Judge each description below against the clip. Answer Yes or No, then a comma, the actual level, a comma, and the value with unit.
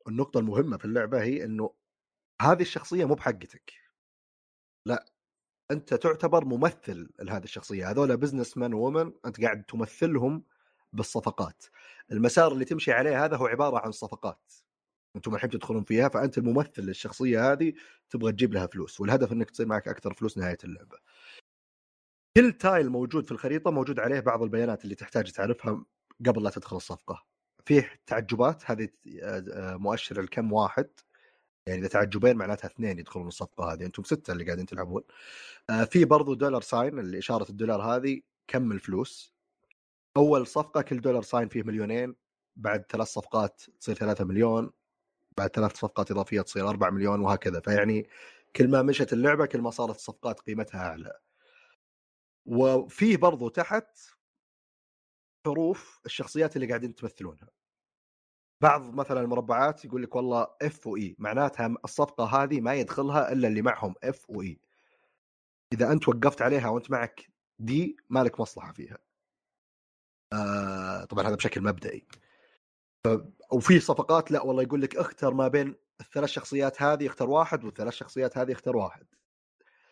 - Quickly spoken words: Yes, fast, 145 wpm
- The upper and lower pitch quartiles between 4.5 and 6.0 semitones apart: Yes, average, 5.3 semitones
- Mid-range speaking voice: No, low, 120 Hz